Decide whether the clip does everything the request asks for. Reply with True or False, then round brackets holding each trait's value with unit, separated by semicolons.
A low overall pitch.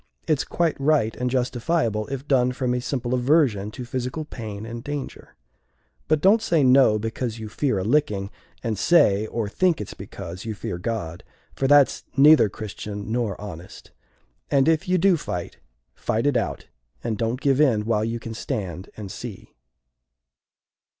True (120 Hz)